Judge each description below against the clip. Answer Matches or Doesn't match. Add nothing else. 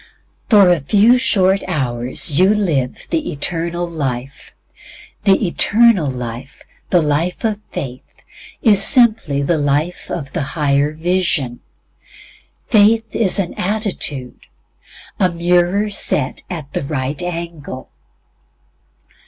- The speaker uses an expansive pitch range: Matches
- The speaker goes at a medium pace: Doesn't match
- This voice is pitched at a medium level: Matches